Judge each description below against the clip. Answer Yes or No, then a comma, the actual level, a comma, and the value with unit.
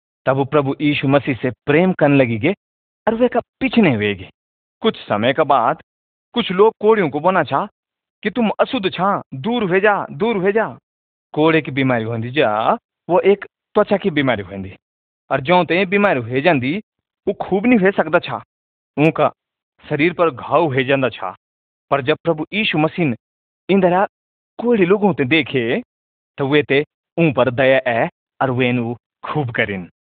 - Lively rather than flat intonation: Yes, wide, 7.9 semitones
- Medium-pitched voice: Yes, medium, 150 Hz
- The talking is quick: No, average, 160 wpm